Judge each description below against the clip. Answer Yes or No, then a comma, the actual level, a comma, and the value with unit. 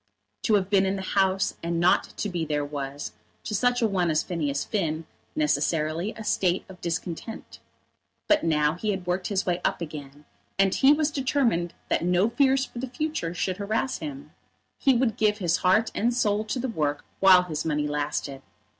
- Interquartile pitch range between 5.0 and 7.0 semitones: Yes, wide, 5.5 semitones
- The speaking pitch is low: No, medium, 185 Hz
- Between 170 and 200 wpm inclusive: Yes, average, 190 wpm